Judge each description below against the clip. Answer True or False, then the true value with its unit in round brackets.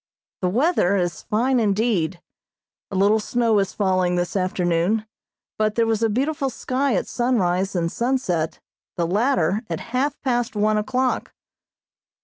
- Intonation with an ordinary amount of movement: True (4.9 semitones)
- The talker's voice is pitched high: True (215 Hz)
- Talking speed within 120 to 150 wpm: True (140 wpm)